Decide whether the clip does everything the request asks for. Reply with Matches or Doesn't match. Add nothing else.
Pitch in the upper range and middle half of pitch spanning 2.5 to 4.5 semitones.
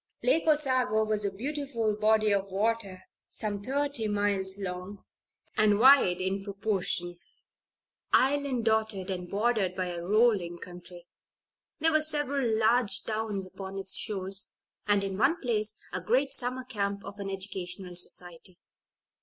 Matches